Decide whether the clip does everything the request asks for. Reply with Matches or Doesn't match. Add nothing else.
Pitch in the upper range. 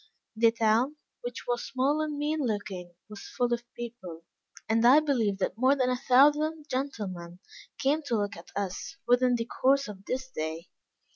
Matches